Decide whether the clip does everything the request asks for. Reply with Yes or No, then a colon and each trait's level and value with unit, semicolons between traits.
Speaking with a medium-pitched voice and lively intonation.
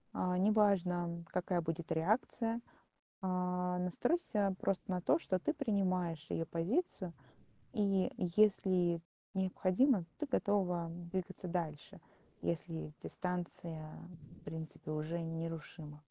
No: medium, 180 Hz; average, 3.2 semitones